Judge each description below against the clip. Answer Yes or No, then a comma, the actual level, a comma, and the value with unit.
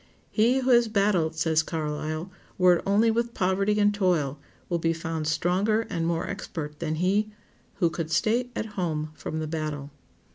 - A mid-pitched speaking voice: Yes, medium, 175 Hz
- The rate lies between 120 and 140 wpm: No, average, 175 wpm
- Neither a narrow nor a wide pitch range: Yes, average, 4.6 semitones